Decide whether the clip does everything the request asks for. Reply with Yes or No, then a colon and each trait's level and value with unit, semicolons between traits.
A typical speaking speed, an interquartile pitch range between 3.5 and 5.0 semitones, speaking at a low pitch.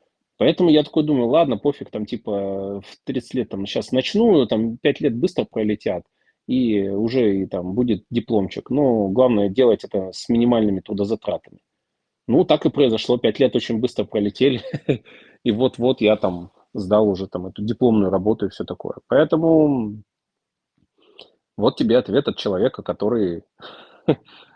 Yes: average, 150 wpm; average, 4.2 semitones; low, 110 Hz